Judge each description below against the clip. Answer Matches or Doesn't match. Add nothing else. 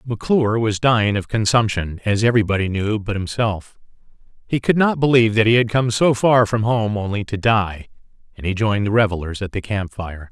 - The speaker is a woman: Doesn't match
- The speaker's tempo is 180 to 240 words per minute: Matches